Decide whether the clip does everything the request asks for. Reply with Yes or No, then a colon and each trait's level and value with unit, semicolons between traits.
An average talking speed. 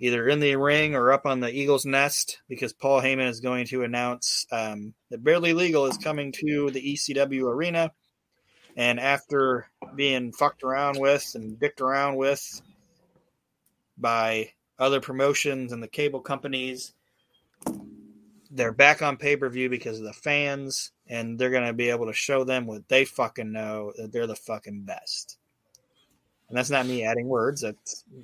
Yes: average, 170 wpm